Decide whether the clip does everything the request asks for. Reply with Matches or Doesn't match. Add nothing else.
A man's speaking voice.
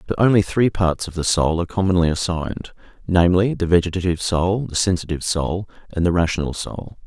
Matches